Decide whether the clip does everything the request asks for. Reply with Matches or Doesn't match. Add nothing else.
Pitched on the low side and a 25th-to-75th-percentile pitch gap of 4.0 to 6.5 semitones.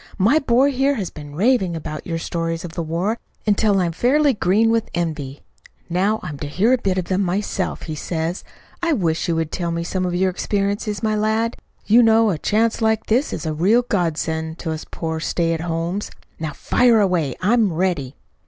Doesn't match